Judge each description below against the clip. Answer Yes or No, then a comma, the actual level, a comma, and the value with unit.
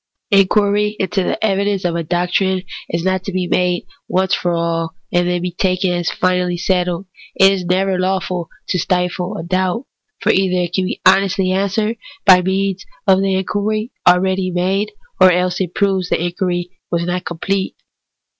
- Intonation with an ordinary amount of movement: No, narrow, 1.5 semitones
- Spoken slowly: No, average, 175 wpm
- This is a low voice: No, medium, 185 Hz